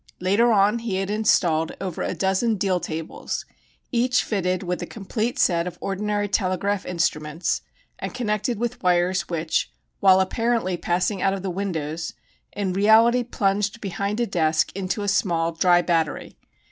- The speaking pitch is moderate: No, high, 195 Hz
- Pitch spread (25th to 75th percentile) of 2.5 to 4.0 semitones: Yes, average, 3.1 semitones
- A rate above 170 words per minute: No, average, 155 wpm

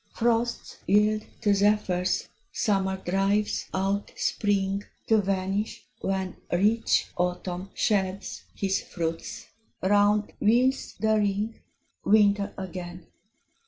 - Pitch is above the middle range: Yes, high, 200 Hz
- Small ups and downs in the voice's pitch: Yes, narrow, 1.8 semitones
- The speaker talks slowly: Yes, slow, 95 wpm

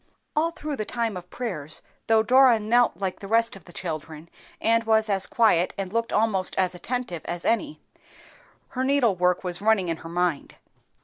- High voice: Yes, high, 210 Hz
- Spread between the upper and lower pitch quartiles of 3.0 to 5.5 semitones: Yes, average, 4.5 semitones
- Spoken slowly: No, average, 180 wpm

